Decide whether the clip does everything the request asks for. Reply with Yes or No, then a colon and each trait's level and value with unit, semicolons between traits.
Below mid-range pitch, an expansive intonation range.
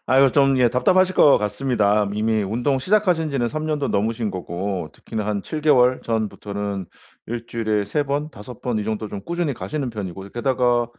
No: low, 120 Hz; average, 4.9 semitones